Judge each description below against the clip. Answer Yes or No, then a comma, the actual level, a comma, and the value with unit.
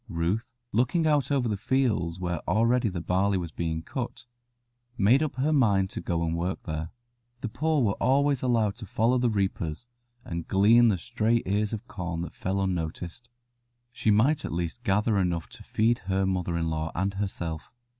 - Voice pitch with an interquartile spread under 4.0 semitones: No, wide, 5.5 semitones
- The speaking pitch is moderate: No, low, 100 Hz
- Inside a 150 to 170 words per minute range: No, average, 185 wpm